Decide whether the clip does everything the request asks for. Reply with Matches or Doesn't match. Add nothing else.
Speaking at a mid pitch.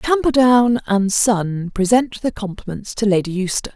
Doesn't match